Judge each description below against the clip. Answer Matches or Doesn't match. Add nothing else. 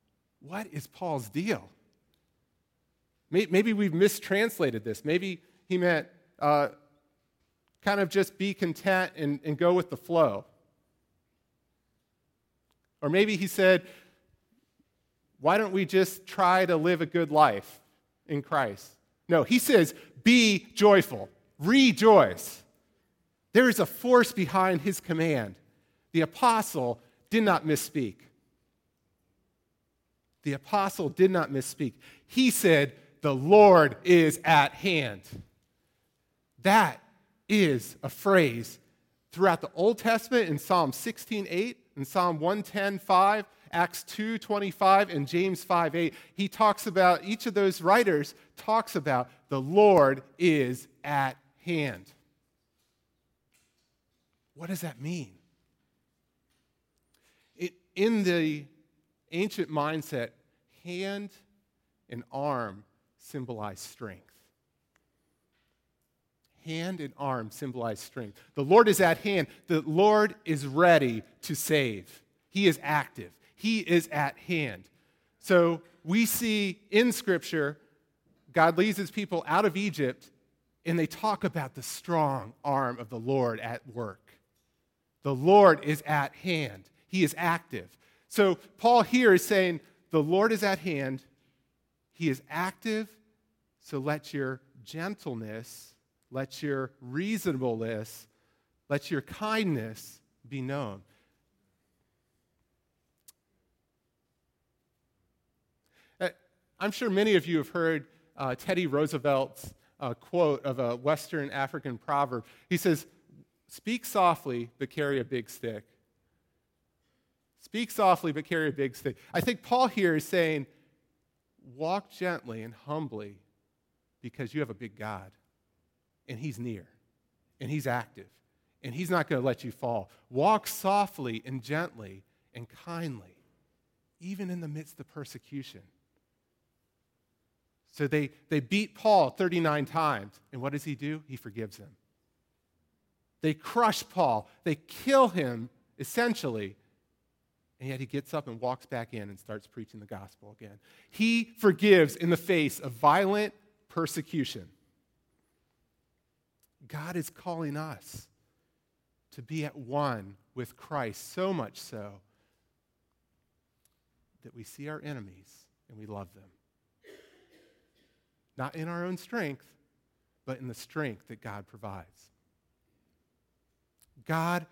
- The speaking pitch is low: Doesn't match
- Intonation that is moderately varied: Doesn't match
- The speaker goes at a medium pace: Doesn't match